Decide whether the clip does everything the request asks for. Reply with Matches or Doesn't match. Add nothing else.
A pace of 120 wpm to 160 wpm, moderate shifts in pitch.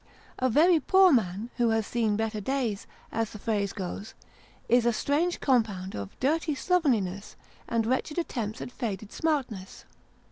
Matches